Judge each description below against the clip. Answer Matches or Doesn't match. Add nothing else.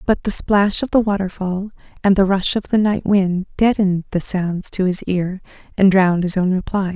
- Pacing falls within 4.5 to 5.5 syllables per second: Matches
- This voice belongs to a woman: Matches